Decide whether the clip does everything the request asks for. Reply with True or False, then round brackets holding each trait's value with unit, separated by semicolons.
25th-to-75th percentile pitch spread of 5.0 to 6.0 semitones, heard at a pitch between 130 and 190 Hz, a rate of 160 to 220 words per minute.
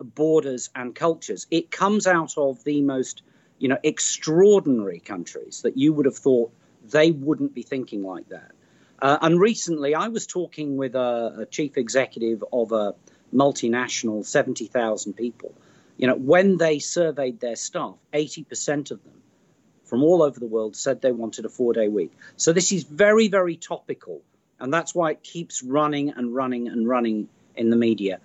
True (5.3 semitones; 140 Hz; 170 wpm)